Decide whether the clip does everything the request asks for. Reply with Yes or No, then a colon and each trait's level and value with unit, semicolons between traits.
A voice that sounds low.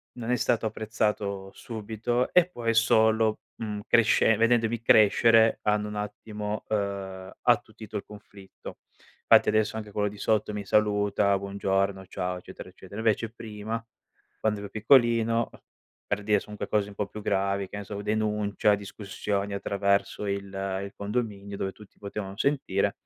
Yes: low, 105 Hz